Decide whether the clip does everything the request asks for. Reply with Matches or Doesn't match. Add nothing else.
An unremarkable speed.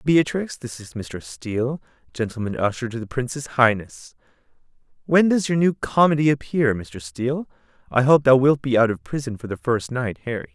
Matches